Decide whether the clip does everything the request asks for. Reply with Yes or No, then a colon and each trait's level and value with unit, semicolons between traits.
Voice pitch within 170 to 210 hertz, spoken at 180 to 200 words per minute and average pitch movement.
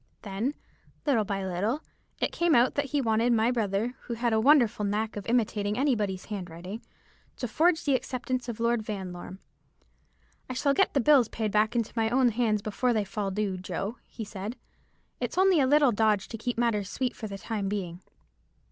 No: high, 225 Hz; average, 190 wpm; average, 3.6 semitones